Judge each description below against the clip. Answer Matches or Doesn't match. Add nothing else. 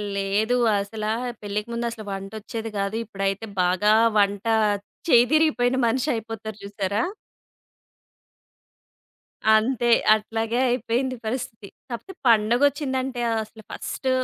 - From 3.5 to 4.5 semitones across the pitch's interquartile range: Doesn't match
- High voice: Matches